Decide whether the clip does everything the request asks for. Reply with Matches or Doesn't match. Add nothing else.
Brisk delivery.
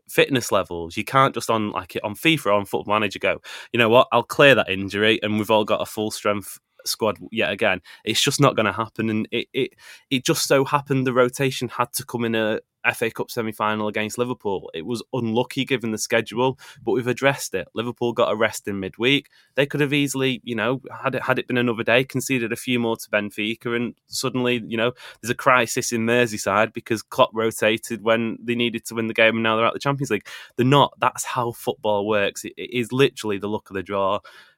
Matches